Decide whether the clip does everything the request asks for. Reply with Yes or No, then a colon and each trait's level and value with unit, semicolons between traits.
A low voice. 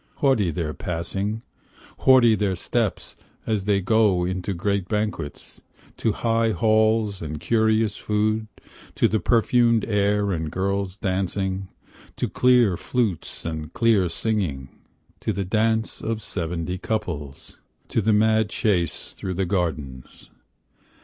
Yes: low, 100 Hz